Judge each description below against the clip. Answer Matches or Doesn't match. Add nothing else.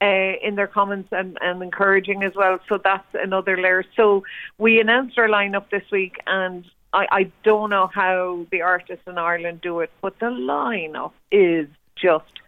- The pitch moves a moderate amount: Doesn't match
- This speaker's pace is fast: Doesn't match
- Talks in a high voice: Matches